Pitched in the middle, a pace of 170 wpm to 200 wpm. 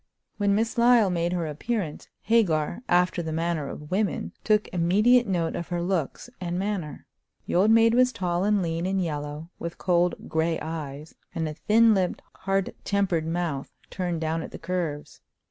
Yes: medium, 175 Hz; average, 175 wpm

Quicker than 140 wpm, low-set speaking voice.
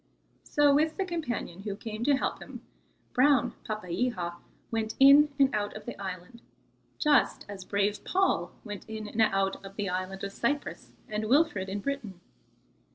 No: average, 160 wpm; high, 215 Hz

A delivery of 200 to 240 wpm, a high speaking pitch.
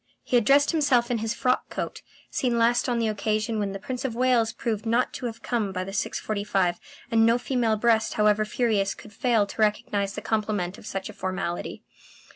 Yes: fast, 205 wpm; high, 220 Hz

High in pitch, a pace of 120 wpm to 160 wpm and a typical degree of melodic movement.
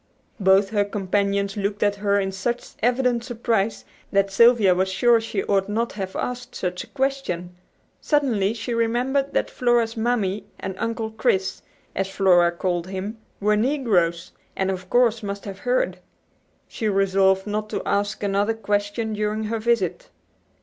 Yes: high, 205 Hz; average, 155 wpm; average, 3.1 semitones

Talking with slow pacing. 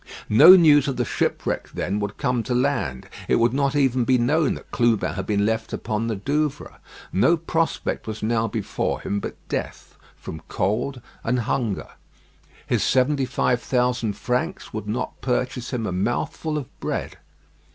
No: average, 165 wpm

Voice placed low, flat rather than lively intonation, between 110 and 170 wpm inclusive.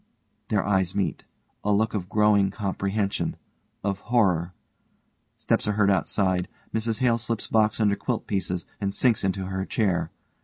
Yes: low, 100 Hz; narrow, 2.2 semitones; average, 150 wpm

